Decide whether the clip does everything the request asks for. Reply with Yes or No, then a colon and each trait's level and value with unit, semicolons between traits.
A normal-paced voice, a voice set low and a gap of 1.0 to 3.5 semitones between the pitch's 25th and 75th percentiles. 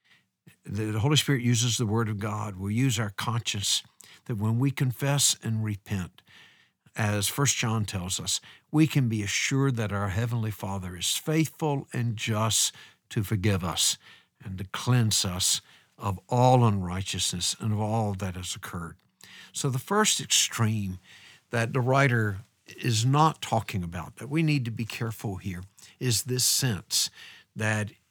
No: average, 155 wpm; low, 110 Hz; average, 3.9 semitones